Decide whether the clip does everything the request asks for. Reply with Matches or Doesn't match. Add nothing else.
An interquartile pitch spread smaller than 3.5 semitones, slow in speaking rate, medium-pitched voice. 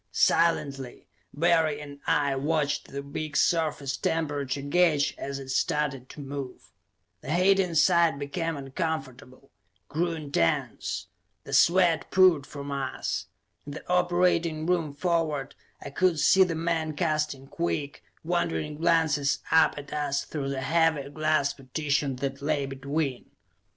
Matches